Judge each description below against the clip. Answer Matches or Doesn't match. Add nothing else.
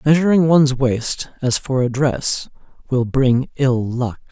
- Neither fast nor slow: Matches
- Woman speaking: Doesn't match